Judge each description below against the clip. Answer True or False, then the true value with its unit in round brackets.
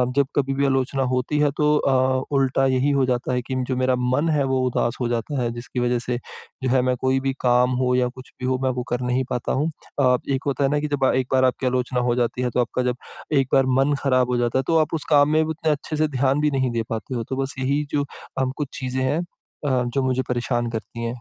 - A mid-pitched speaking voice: False (130 Hz)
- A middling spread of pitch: False (1.9 semitones)